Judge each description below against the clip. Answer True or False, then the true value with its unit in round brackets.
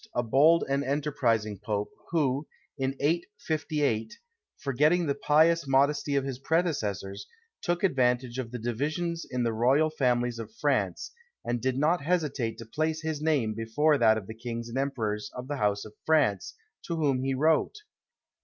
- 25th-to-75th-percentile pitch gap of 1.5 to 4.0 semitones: False (4.9 semitones)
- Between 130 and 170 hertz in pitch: True (135 Hz)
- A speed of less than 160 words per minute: False (165 wpm)